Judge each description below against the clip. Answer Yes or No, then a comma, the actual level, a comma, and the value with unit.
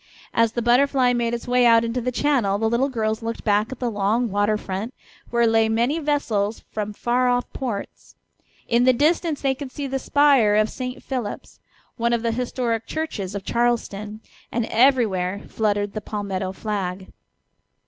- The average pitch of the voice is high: Yes, high, 230 Hz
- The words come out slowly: No, average, 175 wpm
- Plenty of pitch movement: No, average, 3.1 semitones